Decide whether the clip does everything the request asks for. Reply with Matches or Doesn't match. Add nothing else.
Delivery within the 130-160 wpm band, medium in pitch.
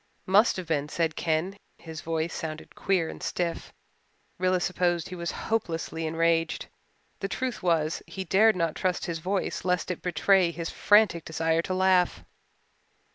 Matches